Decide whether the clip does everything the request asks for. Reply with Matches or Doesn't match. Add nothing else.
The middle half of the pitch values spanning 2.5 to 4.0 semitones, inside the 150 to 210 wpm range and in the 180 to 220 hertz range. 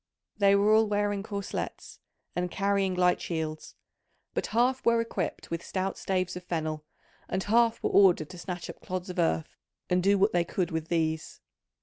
Matches